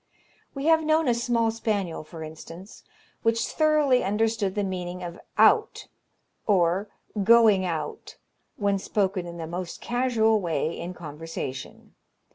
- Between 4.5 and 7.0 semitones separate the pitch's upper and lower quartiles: Yes, average, 5.1 semitones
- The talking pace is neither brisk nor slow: No, slow, 130 wpm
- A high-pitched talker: Yes, high, 200 Hz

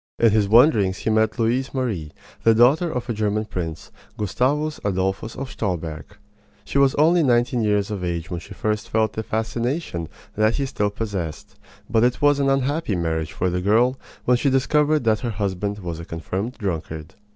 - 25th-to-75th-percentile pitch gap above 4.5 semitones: Yes, average, 5.1 semitones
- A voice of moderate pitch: No, low, 110 Hz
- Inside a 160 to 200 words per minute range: Yes, average, 185 wpm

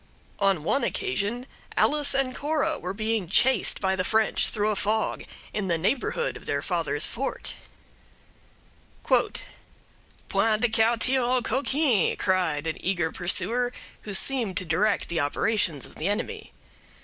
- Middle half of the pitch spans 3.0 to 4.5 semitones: No, average, 5.1 semitones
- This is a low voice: No, high, 215 Hz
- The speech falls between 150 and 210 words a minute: No, average, 140 wpm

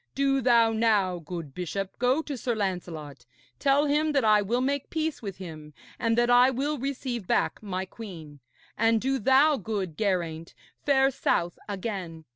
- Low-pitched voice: No, high, 220 Hz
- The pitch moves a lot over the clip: Yes, wide, 6.7 semitones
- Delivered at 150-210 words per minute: Yes, average, 165 wpm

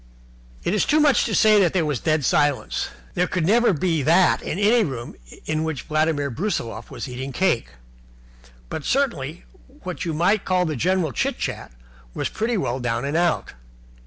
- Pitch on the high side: No, medium, 165 Hz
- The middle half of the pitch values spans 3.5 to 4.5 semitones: No, average, 5.3 semitones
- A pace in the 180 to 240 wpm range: Yes, average, 185 wpm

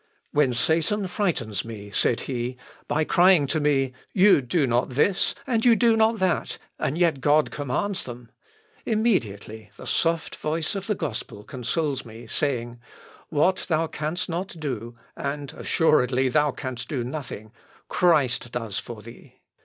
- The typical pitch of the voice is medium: Yes, medium, 145 Hz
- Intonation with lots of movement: Yes, wide, 6.1 semitones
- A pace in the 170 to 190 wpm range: No, average, 150 wpm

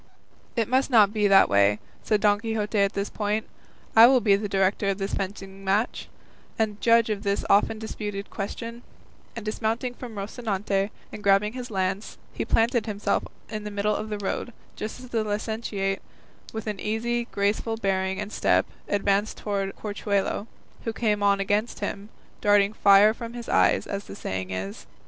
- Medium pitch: No, high, 210 Hz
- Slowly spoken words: No, average, 175 wpm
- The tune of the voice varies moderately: No, narrow, 2.0 semitones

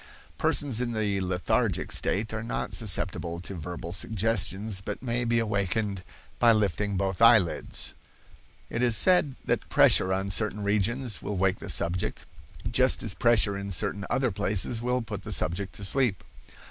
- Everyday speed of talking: Yes, average, 160 wpm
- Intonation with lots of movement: No, average, 3.3 semitones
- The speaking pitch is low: Yes, low, 105 Hz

